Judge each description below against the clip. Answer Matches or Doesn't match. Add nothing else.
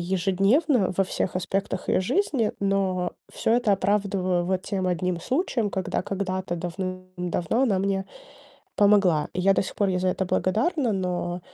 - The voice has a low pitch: Doesn't match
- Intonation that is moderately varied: Doesn't match